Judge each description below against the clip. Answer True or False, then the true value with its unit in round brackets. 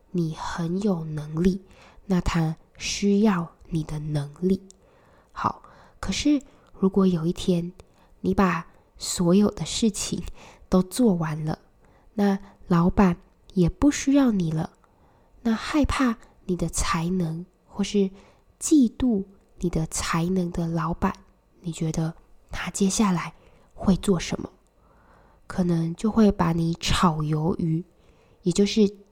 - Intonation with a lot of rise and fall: False (3.3 semitones)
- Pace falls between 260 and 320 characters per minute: False (170 characters per minute)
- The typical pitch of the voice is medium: True (180 Hz)